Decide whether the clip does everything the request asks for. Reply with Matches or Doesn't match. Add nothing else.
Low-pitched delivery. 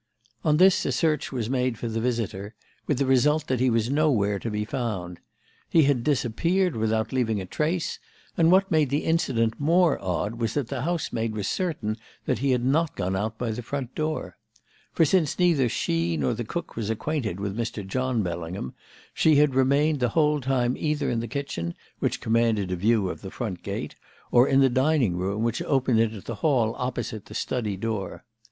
Matches